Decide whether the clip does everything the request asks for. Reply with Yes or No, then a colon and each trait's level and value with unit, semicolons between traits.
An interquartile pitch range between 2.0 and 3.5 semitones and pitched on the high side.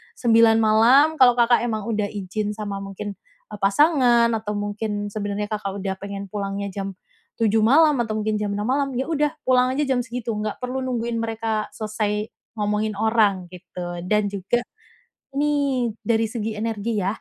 Yes: narrow, 2.6 semitones; high, 215 Hz